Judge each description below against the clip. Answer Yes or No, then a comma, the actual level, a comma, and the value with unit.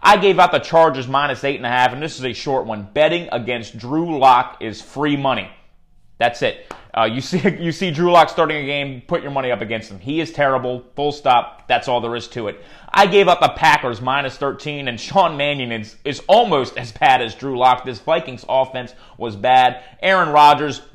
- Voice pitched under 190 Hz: Yes, low, 135 Hz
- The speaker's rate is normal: No, fast, 220 wpm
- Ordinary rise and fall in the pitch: Yes, average, 4.0 semitones